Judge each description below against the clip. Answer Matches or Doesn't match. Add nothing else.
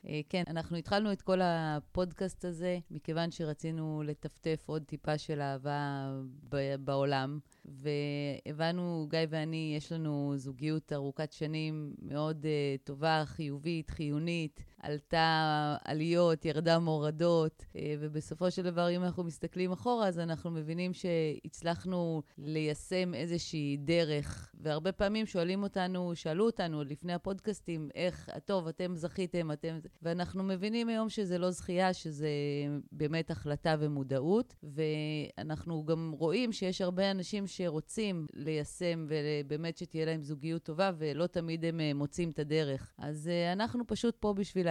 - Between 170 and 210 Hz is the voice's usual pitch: Doesn't match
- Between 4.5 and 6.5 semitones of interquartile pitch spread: Doesn't match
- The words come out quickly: Doesn't match